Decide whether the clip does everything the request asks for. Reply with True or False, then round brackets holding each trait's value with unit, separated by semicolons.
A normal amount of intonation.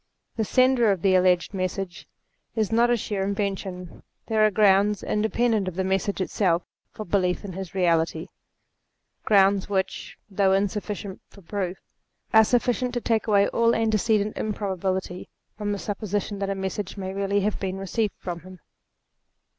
False (2.2 semitones)